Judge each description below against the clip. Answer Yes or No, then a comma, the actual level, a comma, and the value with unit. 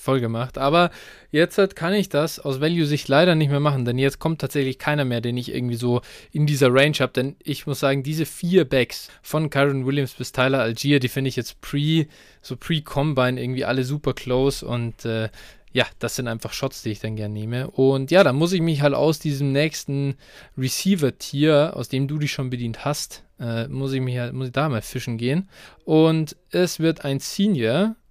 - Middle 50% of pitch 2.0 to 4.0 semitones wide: Yes, average, 3.4 semitones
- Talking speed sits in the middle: No, fast, 210 wpm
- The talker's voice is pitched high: No, medium, 140 Hz